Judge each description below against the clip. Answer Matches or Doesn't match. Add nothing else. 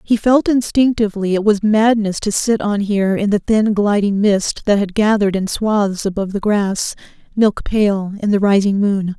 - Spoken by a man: Doesn't match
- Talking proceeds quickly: Doesn't match